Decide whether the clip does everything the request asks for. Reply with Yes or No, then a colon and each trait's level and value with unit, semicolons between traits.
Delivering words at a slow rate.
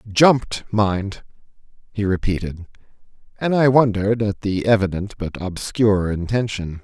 Yes: slow, 105 wpm